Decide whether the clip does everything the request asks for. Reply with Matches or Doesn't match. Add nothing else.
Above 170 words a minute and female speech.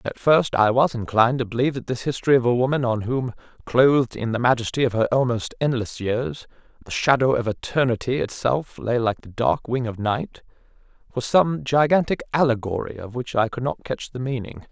Doesn't match